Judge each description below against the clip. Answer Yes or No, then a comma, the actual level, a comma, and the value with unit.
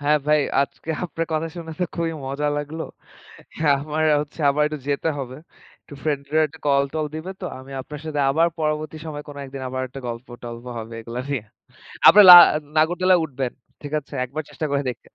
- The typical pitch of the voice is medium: Yes, medium, 150 Hz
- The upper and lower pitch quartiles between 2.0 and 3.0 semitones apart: Yes, narrow, 2.4 semitones